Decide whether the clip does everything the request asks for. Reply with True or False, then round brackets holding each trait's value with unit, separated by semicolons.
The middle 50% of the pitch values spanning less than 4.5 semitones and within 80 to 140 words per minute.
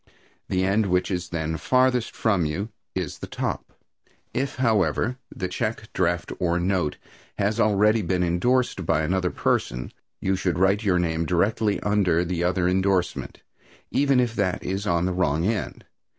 False (3.4 semitones; 160 wpm)